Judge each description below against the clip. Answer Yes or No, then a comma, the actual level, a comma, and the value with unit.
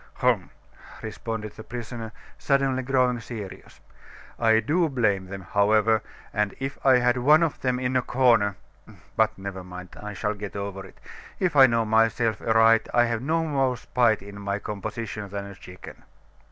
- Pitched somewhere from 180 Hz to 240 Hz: No, low, 115 Hz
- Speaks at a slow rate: No, average, 165 wpm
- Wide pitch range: No, average, 3.7 semitones